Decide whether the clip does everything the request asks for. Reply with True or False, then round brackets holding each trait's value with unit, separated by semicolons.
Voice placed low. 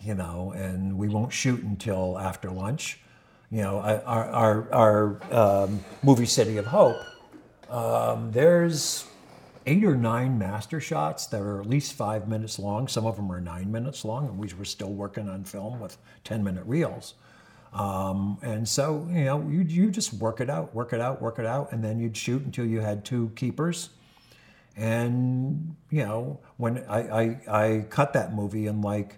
True (115 Hz)